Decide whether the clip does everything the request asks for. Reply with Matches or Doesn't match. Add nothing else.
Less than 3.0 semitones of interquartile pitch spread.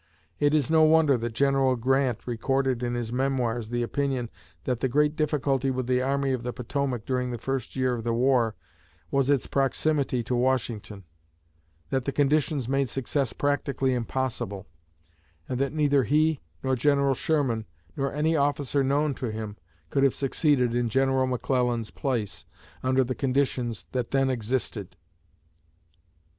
Matches